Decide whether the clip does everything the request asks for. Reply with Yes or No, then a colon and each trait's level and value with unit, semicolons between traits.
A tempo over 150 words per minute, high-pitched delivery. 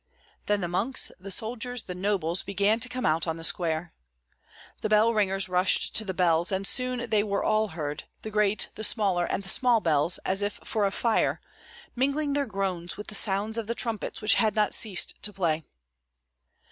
Yes: average, 195 wpm; high, 205 Hz